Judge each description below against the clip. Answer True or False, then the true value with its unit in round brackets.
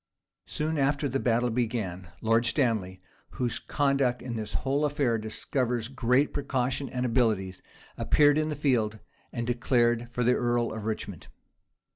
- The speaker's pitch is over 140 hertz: False (120 Hz)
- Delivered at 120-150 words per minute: True (145 wpm)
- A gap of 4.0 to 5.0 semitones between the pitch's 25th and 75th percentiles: False (3.2 semitones)